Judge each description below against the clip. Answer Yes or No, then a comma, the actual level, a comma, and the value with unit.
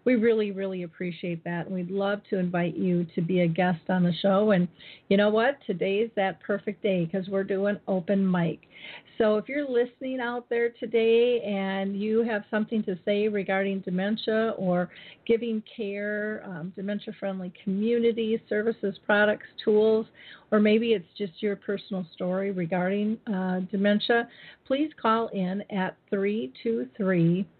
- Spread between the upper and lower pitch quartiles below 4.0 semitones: Yes, average, 2.9 semitones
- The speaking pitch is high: Yes, high, 205 Hz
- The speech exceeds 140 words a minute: Yes, average, 155 wpm